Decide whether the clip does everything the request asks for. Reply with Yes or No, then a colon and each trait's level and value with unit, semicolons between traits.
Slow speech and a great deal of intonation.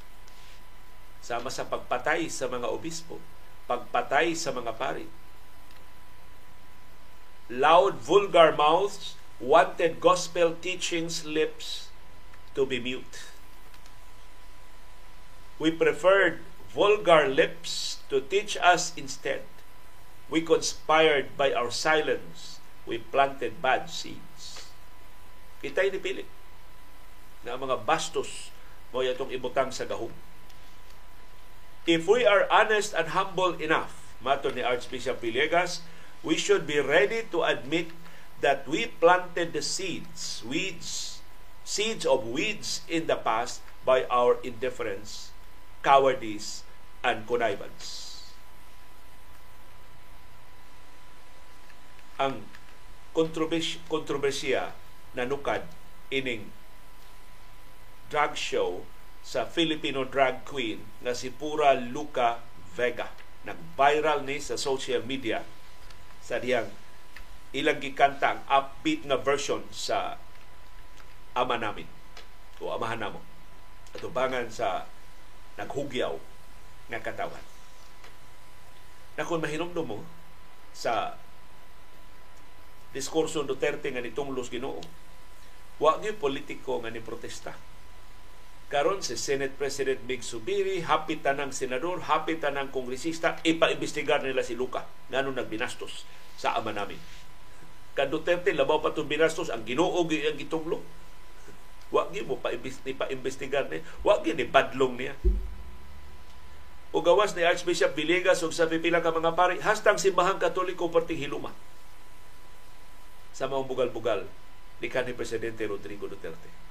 Yes: slow, 105 wpm; wide, 7.8 semitones